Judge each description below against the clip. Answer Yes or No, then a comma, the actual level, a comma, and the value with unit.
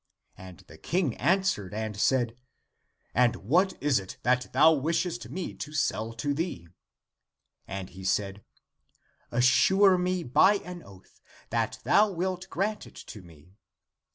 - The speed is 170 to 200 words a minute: No, average, 155 wpm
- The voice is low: Yes, low, 130 Hz